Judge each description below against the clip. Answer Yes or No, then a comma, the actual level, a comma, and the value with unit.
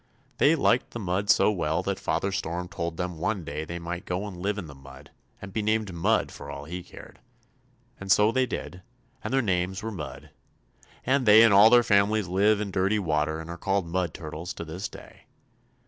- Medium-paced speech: No, fast, 210 wpm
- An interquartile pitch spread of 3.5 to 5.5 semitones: Yes, average, 3.9 semitones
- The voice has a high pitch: No, very low, 95 Hz